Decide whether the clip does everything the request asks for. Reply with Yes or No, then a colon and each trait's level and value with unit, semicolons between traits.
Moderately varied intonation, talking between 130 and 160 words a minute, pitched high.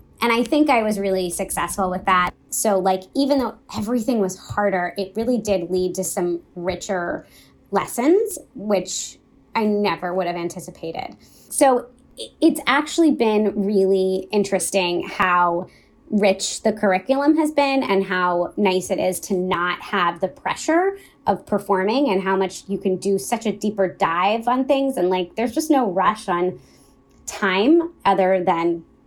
Yes: average, 4.6 semitones; average, 155 wpm; high, 195 Hz